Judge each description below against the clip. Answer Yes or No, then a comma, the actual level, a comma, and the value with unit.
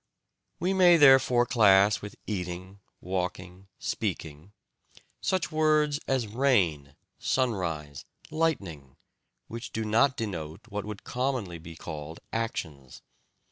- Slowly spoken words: Yes, slow, 105 wpm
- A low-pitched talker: Yes, low, 100 Hz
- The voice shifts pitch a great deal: Yes, wide, 7.3 semitones